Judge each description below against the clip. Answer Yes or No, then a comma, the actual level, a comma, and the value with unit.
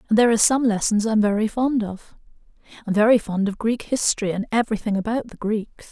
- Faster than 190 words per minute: Yes, fast, 205 wpm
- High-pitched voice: Yes, high, 220 Hz